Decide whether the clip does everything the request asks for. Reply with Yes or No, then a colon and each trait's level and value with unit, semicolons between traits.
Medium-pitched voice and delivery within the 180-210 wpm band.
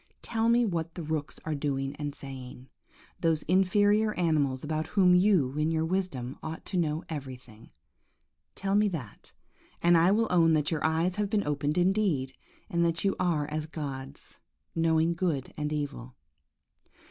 No: medium, 160 Hz; average, 160 wpm